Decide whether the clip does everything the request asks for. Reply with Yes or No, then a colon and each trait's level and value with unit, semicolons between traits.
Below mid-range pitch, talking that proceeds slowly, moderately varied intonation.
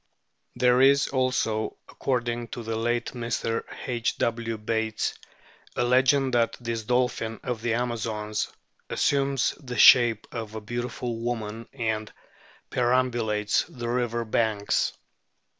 No: low, 120 Hz; slow, 125 wpm; narrow, 1.9 semitones